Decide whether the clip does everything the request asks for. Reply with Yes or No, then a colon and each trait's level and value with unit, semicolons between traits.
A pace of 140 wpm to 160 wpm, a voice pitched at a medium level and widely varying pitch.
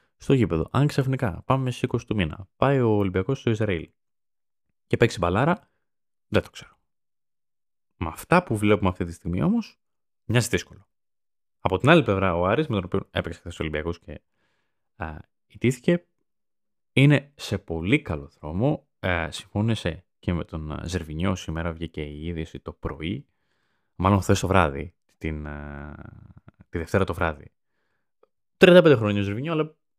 No: average, 150 wpm; very low, 95 Hz; wide, 6.5 semitones